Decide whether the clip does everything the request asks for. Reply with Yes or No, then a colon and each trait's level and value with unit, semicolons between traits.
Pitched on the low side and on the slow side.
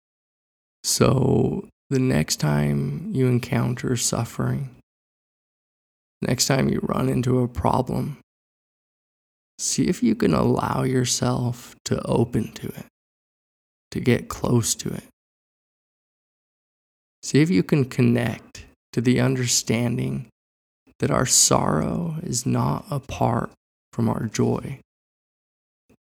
Yes: low, 120 Hz; slow, 105 wpm